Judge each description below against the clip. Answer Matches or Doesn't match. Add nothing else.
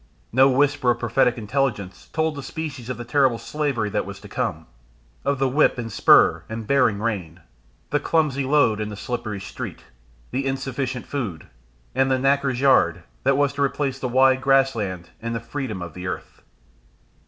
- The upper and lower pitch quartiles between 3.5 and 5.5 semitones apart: Matches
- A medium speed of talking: Matches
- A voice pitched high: Doesn't match